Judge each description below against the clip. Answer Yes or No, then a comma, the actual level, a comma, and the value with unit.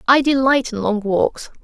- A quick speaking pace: No, average, 185 wpm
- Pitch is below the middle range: No, very high, 250 Hz